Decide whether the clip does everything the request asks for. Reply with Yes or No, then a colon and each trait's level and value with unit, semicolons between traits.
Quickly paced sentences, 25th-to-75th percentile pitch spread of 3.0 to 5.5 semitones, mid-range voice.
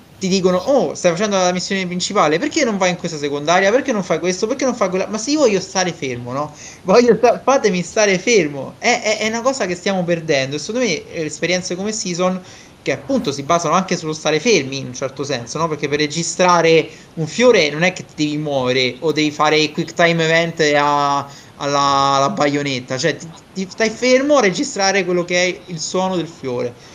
Yes: fast, 220 wpm; average, 4.6 semitones; medium, 175 Hz